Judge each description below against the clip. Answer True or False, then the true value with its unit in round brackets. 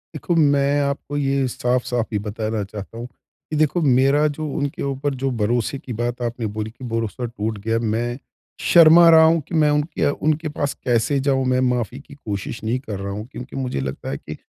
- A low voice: True (125 Hz)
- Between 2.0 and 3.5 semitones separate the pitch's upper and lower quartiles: False (4.1 semitones)